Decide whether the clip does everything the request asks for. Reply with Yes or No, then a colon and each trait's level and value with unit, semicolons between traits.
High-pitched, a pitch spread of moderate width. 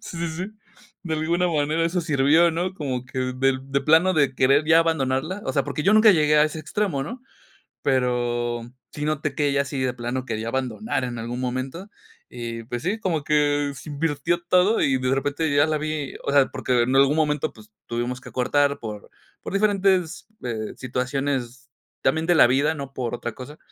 No: medium, 145 Hz; average, 3.8 semitones